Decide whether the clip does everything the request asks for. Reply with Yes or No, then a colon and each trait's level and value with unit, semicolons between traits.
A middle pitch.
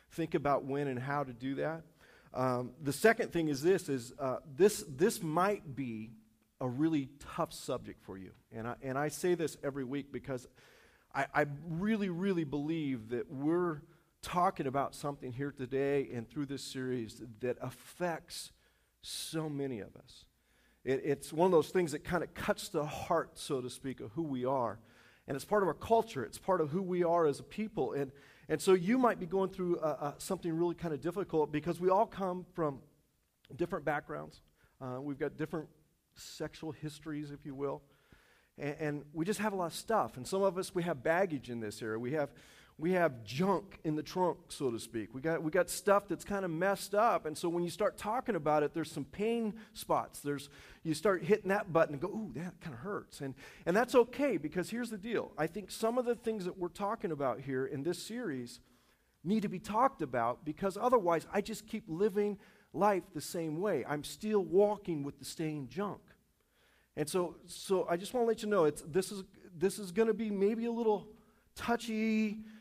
Yes: medium, 165 Hz